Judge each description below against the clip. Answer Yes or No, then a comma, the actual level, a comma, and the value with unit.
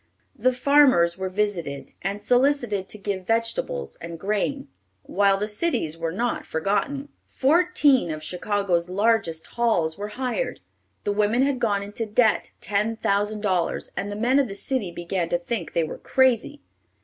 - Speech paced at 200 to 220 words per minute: No, average, 160 wpm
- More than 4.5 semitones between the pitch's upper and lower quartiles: Yes, average, 5.0 semitones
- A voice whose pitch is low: No, high, 205 Hz